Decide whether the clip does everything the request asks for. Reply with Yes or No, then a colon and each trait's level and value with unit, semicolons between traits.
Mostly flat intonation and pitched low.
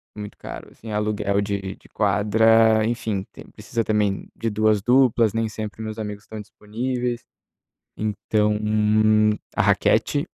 Yes: narrow, 1.4 semitones; low, 110 Hz